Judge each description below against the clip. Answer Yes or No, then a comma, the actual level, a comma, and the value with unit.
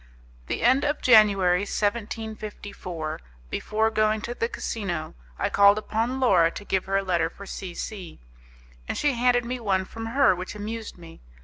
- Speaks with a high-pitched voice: Yes, high, 210 Hz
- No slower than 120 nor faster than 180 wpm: Yes, average, 170 wpm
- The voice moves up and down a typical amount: Yes, average, 3.4 semitones